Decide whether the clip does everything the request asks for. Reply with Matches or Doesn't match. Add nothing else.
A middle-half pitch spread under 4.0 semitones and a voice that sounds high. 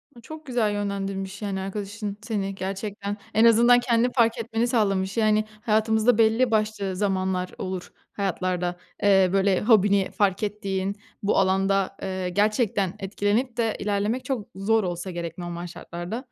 Matches